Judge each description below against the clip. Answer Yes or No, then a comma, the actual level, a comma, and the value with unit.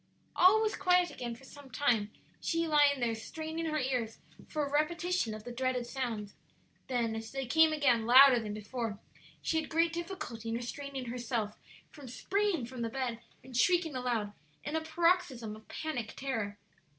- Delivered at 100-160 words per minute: No, average, 175 wpm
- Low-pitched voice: No, very high, 260 Hz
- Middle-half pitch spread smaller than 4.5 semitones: No, wide, 5.5 semitones